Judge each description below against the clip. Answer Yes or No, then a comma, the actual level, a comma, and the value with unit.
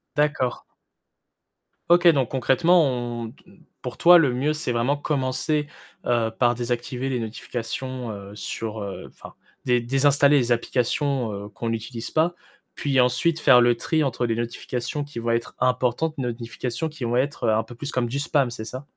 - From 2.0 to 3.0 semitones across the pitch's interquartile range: No, average, 3.4 semitones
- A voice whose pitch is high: No, low, 125 Hz